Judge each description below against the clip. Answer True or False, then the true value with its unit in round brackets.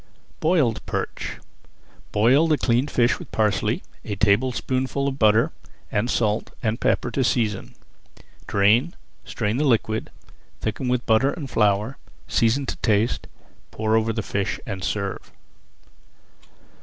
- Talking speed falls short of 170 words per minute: True (135 wpm)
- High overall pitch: False (115 Hz)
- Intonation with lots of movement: False (3.6 semitones)